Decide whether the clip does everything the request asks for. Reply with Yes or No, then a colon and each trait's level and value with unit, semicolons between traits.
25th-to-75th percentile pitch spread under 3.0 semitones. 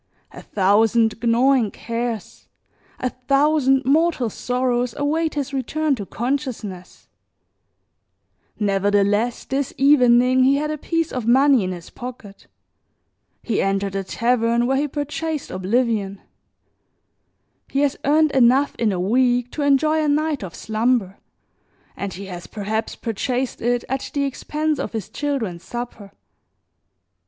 No: average, 4.7 semitones